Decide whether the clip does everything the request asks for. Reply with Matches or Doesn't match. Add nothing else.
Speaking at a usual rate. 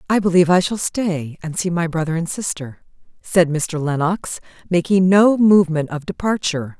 Matches